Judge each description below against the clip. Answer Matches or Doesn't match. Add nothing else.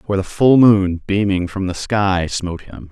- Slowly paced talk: Doesn't match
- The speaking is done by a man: Matches